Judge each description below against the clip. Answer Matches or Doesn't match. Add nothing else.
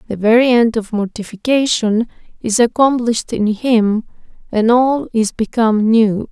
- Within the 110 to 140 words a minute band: Matches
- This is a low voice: Doesn't match